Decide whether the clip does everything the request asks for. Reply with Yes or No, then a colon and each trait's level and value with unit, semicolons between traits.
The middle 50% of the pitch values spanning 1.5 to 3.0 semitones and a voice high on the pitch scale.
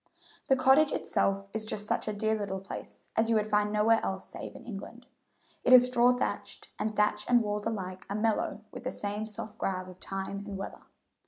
Yes: narrow, 2.4 semitones; high, 210 Hz